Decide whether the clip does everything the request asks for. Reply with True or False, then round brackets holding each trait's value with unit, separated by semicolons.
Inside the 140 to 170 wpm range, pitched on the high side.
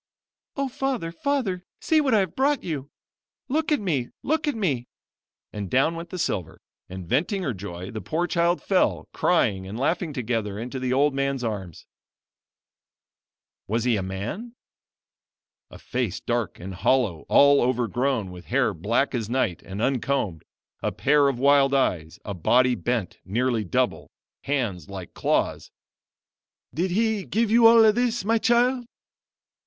False (155 wpm; 135 Hz)